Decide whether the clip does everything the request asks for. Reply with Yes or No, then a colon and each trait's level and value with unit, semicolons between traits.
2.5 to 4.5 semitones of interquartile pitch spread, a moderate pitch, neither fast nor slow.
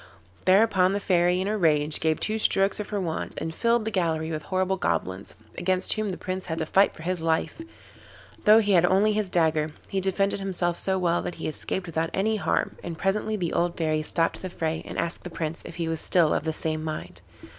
No: average, 3.2 semitones; medium, 180 Hz; fast, 225 wpm